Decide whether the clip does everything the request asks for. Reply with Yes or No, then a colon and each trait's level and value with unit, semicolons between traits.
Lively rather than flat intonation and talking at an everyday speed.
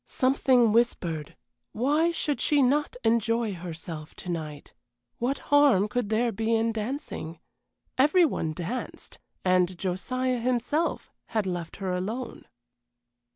No: wide, 6.1 semitones; slow, 120 wpm